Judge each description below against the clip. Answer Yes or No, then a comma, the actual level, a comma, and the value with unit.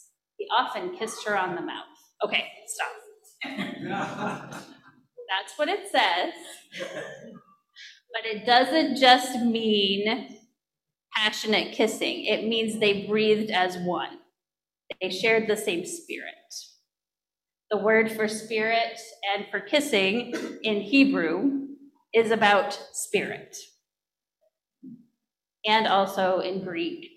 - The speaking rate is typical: No, slow, 105 wpm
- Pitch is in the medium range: No, high, 225 Hz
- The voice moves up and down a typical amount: Yes, average, 4.9 semitones